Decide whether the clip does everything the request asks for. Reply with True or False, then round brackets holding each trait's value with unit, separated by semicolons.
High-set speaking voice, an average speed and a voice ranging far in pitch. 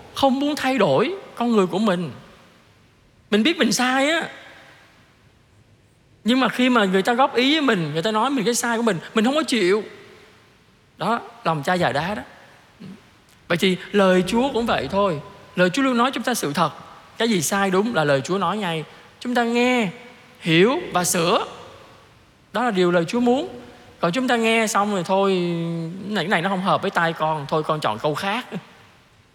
True (200 Hz; 200 wpm; 6.5 semitones)